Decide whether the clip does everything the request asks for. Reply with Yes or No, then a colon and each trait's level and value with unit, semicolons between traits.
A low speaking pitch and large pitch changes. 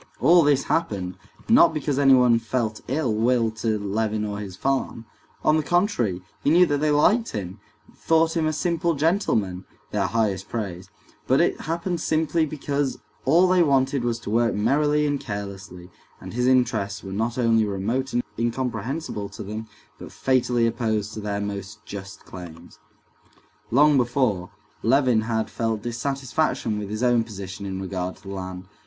Yes: low, 115 Hz; wide, 5.7 semitones